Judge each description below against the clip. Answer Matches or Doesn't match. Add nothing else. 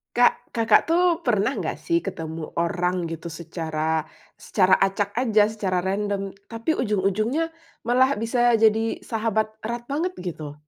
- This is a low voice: Doesn't match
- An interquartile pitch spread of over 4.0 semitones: Matches